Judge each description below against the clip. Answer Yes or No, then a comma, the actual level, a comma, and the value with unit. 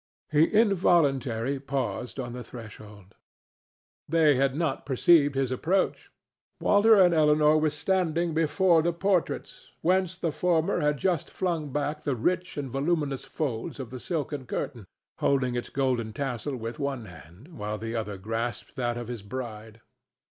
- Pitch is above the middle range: No, medium, 140 Hz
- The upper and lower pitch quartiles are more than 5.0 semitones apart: Yes, wide, 5.4 semitones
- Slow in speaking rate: No, average, 150 wpm